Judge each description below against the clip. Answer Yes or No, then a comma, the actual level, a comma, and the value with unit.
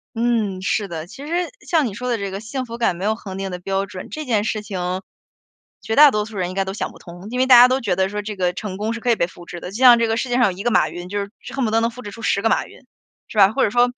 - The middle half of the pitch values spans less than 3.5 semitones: No, average, 3.9 semitones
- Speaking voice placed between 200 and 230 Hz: Yes, high, 210 Hz